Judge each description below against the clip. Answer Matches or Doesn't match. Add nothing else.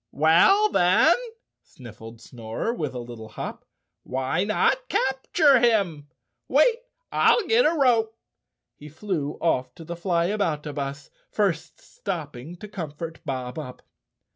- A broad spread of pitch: Matches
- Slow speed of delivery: Matches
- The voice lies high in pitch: Doesn't match